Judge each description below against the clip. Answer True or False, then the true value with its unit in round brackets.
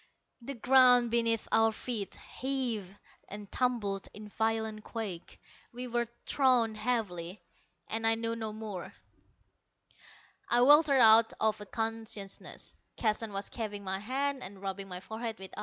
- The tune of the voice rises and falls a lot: False (2.7 semitones)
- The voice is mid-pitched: False (225 Hz)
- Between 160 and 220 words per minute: False (140 wpm)